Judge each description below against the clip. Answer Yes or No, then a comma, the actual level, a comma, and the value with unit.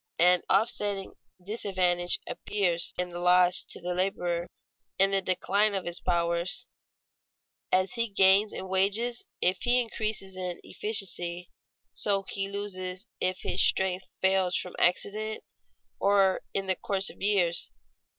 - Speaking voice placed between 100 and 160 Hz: No, high, 190 Hz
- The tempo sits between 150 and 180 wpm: No, slow, 135 wpm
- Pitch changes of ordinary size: No, narrow, 2.0 semitones